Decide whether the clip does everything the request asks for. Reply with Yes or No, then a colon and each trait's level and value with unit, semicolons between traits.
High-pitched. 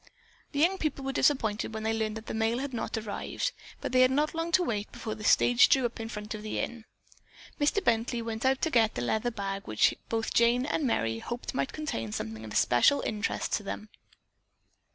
Yes: high, 230 Hz